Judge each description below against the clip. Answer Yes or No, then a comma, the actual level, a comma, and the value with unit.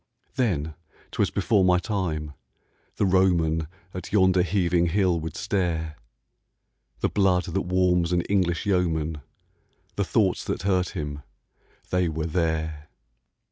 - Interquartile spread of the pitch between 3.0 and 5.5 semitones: No, narrow, 2.5 semitones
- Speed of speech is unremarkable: No, slow, 125 wpm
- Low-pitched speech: Yes, very low, 90 Hz